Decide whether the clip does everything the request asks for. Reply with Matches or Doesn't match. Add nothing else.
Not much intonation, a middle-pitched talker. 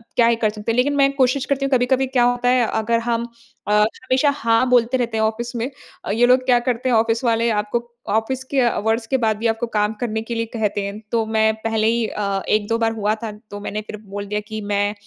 Doesn't match